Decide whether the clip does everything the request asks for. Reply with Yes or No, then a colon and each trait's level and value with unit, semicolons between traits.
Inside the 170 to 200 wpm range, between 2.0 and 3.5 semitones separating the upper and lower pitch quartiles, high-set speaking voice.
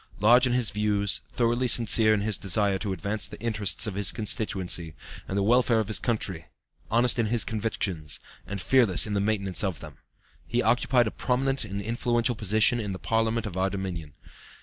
No: average, 190 wpm; average, 3.1 semitones; low, 110 Hz